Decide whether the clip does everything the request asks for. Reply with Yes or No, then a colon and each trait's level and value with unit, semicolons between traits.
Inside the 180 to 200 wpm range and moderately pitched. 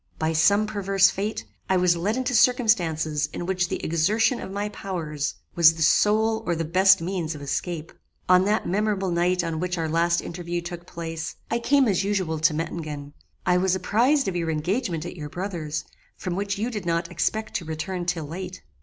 Yes: average, 195 wpm; medium, 180 Hz